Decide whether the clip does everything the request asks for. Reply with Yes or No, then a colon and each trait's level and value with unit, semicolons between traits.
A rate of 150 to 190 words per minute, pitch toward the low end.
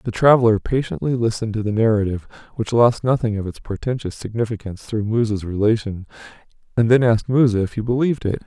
Yes: average, 175 wpm; low, 110 Hz